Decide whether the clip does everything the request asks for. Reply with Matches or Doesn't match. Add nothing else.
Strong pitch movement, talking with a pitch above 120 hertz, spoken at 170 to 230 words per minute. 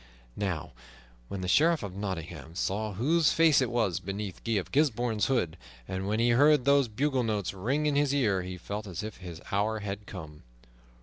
Doesn't match